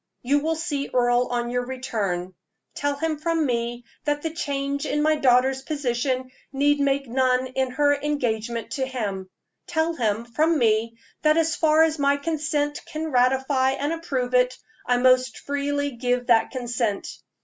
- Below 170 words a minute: Yes, average, 160 wpm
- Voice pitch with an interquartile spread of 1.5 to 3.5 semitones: Yes, average, 3.2 semitones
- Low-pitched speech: No, very high, 265 Hz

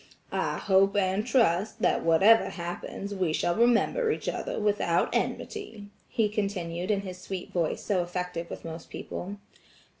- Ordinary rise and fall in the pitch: Yes, average, 3.3 semitones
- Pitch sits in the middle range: No, high, 195 Hz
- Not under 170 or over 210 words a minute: No, average, 150 wpm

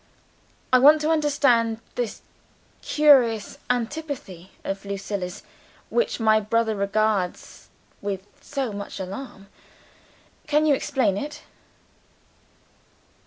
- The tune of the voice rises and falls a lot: Yes, wide, 6.1 semitones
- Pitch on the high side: Yes, high, 230 Hz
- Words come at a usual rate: No, slow, 95 wpm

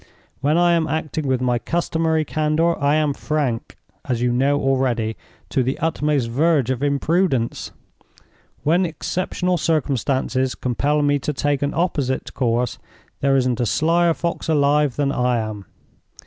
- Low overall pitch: No, medium, 145 Hz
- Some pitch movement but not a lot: Yes, average, 3.7 semitones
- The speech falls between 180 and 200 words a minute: No, average, 150 wpm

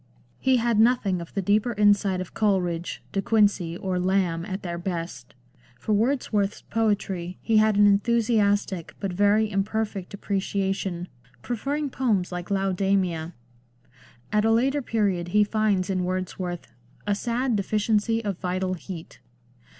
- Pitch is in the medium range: No, high, 200 Hz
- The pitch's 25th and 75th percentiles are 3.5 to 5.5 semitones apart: No, average, 2.9 semitones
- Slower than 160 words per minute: Yes, average, 140 wpm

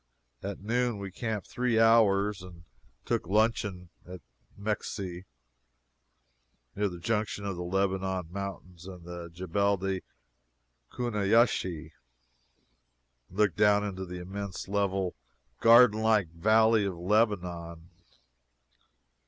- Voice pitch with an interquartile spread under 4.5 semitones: Yes, average, 2.9 semitones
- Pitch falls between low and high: No, low, 100 Hz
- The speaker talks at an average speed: No, slow, 110 wpm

